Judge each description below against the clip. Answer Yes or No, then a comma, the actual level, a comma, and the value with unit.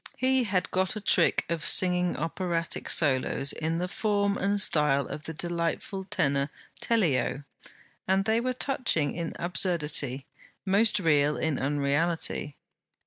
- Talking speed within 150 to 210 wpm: No, slow, 135 wpm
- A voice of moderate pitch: Yes, medium, 170 Hz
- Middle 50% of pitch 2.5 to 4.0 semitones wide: No, average, 4.9 semitones